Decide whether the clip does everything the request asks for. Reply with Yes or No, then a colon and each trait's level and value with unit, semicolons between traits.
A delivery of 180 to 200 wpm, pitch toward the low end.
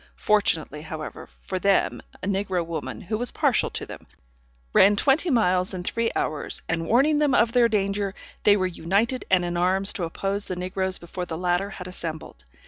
No: average, 185 wpm; high, 190 Hz